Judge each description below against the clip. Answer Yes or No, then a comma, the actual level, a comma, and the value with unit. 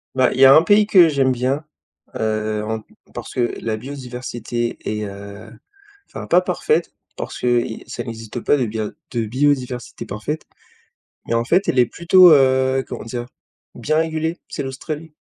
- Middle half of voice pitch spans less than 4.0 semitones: No, average, 4.5 semitones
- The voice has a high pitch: No, low, 125 Hz